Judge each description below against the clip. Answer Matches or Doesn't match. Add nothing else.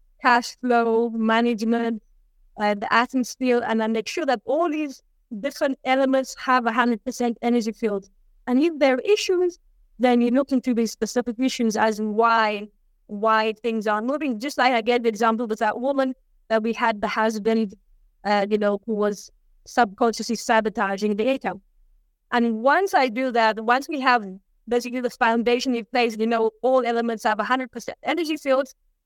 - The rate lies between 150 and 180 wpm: Matches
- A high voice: Matches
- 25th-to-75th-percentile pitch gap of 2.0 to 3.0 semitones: Matches